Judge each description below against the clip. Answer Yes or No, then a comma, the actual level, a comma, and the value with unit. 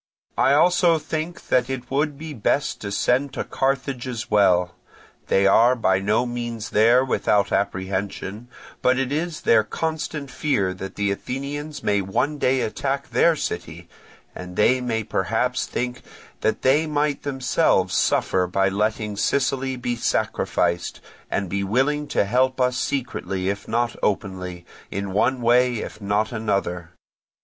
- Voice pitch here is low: Yes, low, 120 Hz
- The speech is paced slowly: No, average, 150 wpm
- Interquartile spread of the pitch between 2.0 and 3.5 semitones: No, average, 5.2 semitones